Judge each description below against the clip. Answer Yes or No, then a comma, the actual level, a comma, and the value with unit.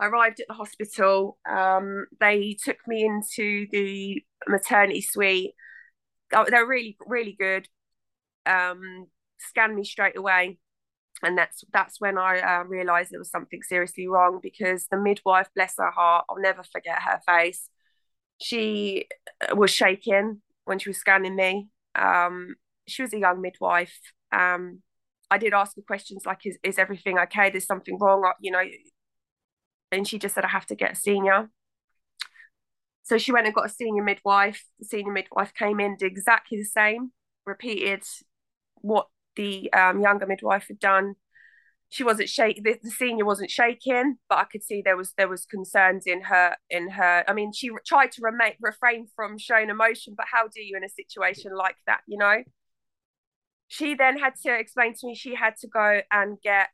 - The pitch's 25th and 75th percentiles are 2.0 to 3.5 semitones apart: Yes, average, 2.8 semitones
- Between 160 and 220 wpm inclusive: Yes, average, 180 wpm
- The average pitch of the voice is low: No, high, 200 Hz